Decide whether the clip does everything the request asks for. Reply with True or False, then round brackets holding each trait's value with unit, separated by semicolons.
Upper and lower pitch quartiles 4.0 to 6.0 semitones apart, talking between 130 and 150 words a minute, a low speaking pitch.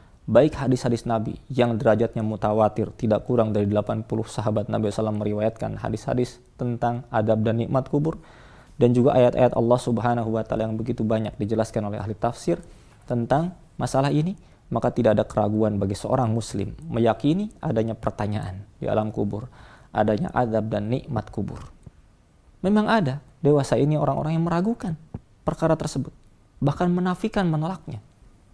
True (4.4 semitones; 140 wpm; 120 Hz)